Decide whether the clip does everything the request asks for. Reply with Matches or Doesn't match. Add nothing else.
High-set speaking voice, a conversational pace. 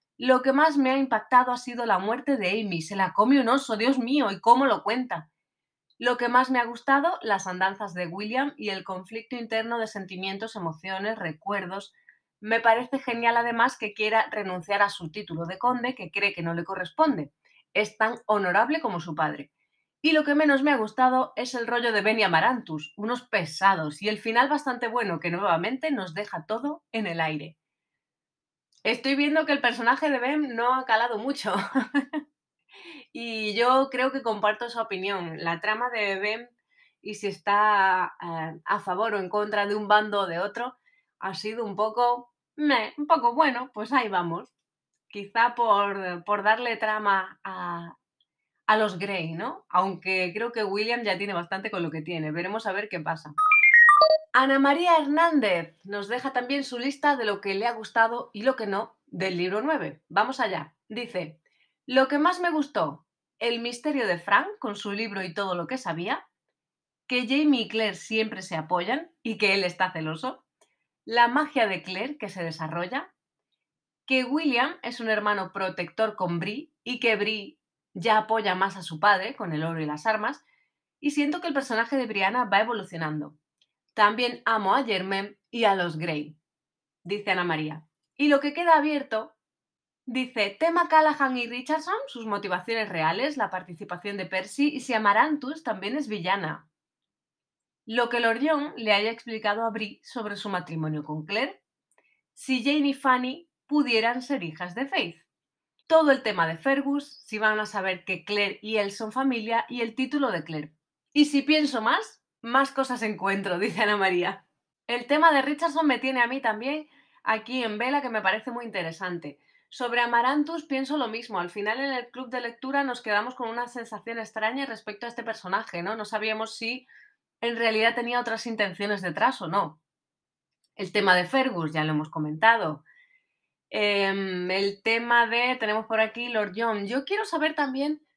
Matches